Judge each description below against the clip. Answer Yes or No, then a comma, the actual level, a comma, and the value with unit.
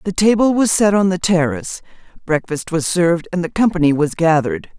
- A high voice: No, medium, 175 Hz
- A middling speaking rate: Yes, average, 190 wpm